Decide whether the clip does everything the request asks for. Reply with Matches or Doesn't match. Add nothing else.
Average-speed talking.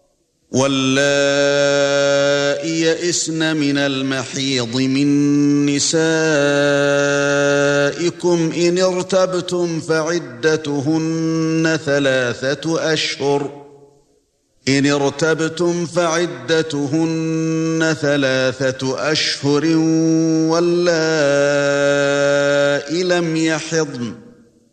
Doesn't match